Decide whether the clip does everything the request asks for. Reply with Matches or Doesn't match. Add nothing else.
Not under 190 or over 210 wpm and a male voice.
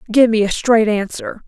Doesn't match